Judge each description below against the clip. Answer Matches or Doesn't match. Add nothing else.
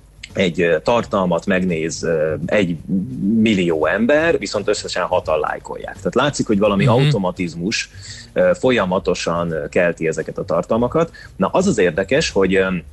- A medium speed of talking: Matches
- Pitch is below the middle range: Matches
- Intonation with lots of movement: Matches